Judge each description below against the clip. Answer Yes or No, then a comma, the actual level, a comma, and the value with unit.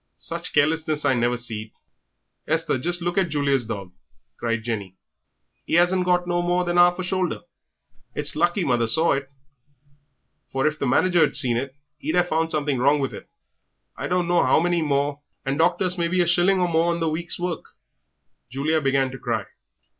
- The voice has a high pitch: No, medium, 155 Hz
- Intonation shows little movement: No, average, 4.6 semitones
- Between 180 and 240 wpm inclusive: Yes, average, 185 wpm